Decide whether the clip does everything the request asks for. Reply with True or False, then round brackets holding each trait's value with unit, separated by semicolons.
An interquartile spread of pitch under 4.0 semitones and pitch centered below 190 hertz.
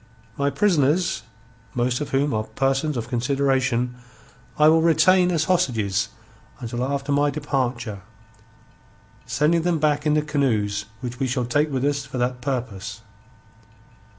True (3.5 semitones; 135 Hz)